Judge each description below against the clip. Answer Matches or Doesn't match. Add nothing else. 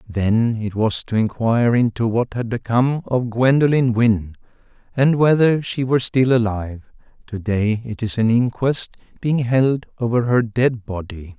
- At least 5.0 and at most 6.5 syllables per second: Doesn't match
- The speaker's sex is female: Doesn't match